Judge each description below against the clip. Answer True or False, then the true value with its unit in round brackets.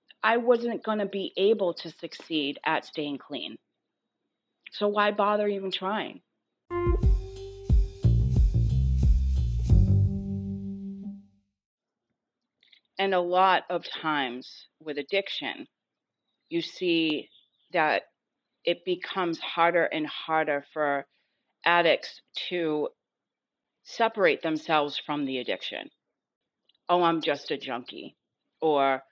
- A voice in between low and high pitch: True (160 Hz)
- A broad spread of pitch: True (8.4 semitones)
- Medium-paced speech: False (95 wpm)